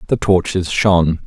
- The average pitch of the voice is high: No, very low, 90 Hz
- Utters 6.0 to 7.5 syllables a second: No, 4.9 syllables/s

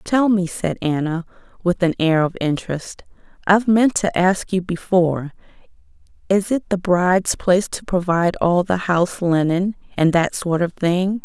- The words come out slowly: No, average, 165 wpm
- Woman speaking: Yes, female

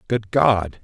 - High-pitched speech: No, low, 110 Hz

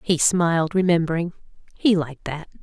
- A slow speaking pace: Yes, slow, 115 wpm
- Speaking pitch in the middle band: Yes, medium, 175 Hz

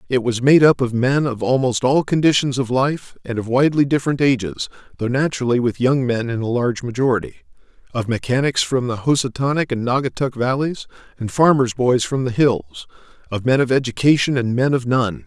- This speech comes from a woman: No, male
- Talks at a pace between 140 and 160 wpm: No, average, 190 wpm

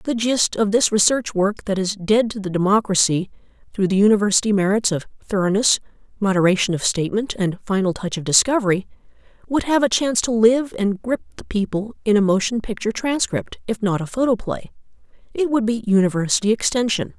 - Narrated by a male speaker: No, female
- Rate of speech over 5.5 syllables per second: Yes, 5.8 syllables/s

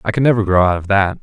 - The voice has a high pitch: No, low, 100 Hz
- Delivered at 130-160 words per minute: No, fast, 345 wpm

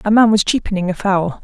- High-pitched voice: Yes, high, 200 Hz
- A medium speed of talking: No, fast, 250 wpm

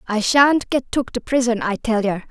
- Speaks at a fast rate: Yes, fast, 235 wpm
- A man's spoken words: No, female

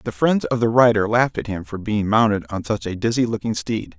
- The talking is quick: Yes, fast, 255 wpm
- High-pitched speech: No, low, 110 Hz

